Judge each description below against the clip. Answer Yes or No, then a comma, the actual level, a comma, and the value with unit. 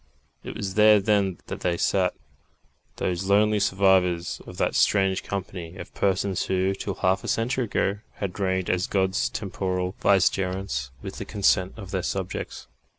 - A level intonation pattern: Yes, narrow, 1.4 semitones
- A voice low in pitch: Yes, very low, 95 Hz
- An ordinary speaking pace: Yes, average, 155 wpm